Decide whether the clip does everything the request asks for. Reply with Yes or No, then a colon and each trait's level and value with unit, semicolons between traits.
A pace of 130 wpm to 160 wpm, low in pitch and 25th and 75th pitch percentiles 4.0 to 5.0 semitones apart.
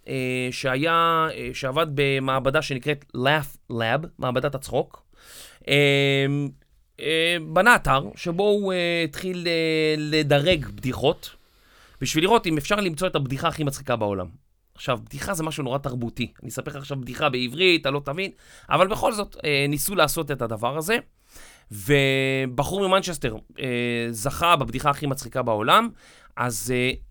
No: average, 145 wpm; medium, 145 Hz; average, 4.3 semitones